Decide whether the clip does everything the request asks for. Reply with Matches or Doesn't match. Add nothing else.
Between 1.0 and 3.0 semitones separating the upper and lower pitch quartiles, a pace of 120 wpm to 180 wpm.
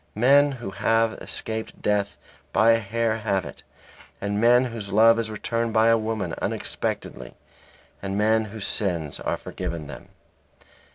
Matches